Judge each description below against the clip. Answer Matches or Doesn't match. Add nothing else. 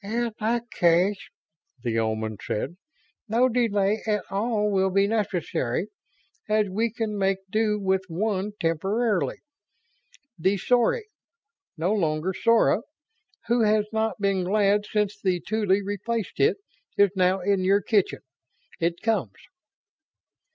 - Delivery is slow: Matches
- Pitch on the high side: Matches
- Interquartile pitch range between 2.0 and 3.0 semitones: Matches